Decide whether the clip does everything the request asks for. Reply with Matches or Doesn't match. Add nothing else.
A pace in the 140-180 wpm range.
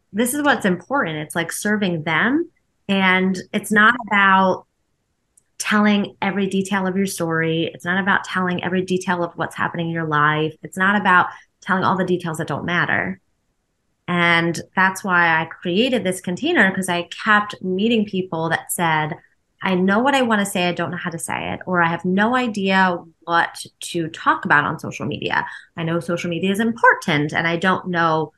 Doesn't match